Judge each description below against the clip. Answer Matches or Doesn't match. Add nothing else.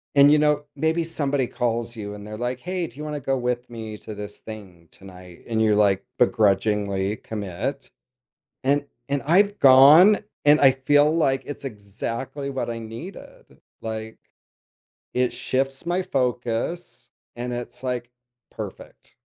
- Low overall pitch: Matches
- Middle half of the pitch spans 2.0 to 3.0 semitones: Doesn't match